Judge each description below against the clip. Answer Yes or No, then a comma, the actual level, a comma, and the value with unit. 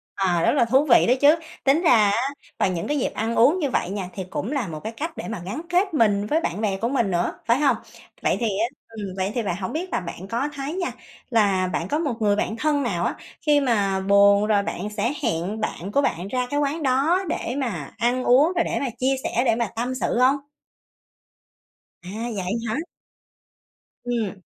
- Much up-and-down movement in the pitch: Yes, wide, 5.7 semitones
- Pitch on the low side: No, high, 230 Hz